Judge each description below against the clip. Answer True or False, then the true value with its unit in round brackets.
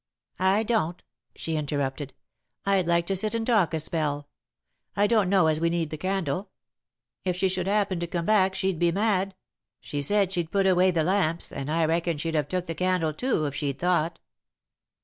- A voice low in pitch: False (175 Hz)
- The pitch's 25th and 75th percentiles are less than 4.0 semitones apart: True (3.3 semitones)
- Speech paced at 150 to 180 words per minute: False (195 wpm)